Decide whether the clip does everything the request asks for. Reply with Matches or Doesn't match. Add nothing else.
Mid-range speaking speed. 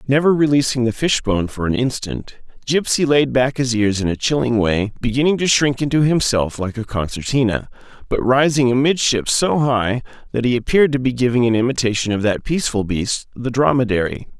Matches